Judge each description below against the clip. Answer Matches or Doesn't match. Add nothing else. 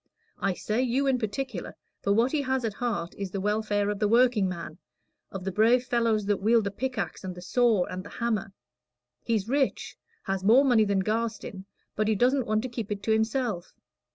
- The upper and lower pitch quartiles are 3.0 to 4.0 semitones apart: Matches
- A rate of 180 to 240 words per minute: Matches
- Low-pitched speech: Doesn't match